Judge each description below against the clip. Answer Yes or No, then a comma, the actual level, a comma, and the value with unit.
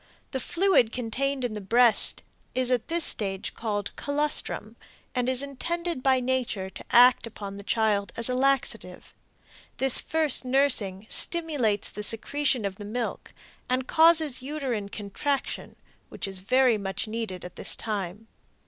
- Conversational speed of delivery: Yes, average, 150 wpm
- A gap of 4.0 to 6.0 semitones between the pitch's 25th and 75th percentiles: Yes, average, 4.7 semitones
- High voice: Yes, high, 245 Hz